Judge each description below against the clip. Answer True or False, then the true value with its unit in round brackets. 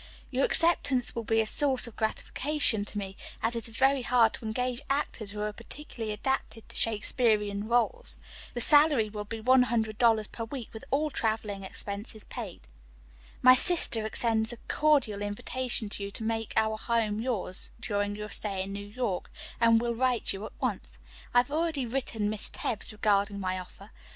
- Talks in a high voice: True (225 Hz)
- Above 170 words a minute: True (180 wpm)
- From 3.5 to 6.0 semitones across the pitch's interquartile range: False (3.1 semitones)